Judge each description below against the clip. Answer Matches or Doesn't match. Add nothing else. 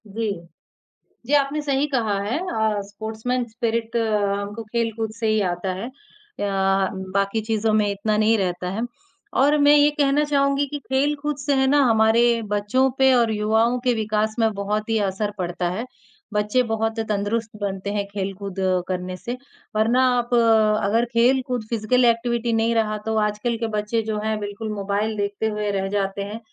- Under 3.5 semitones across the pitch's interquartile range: Matches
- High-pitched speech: Matches